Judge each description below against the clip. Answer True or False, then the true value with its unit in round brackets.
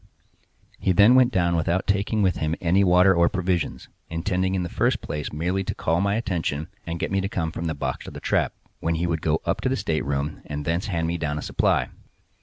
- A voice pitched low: True (85 Hz)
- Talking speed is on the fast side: True (225 wpm)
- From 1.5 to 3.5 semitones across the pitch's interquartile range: True (2.9 semitones)